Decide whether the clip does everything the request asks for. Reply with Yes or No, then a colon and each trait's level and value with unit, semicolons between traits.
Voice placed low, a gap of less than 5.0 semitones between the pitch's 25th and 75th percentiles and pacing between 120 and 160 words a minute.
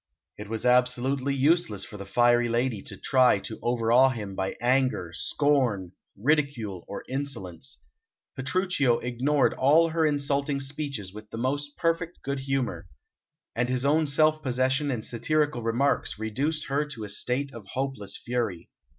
Yes: low, 130 Hz; average, 3.9 semitones; average, 150 wpm